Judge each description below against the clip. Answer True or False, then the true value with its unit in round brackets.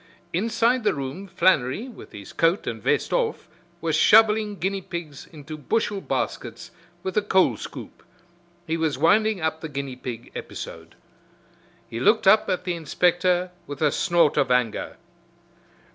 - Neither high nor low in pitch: True (175 Hz)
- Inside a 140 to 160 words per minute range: True (150 wpm)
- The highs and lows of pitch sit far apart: True (5.8 semitones)